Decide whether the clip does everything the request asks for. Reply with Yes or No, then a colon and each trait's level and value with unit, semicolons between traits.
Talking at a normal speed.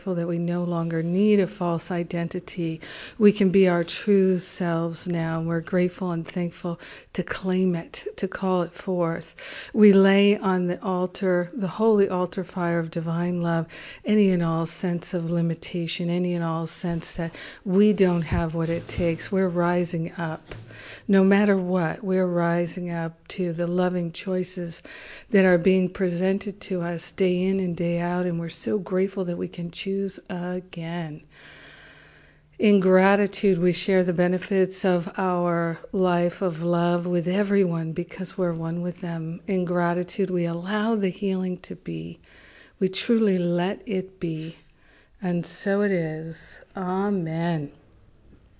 Yes: average, 155 wpm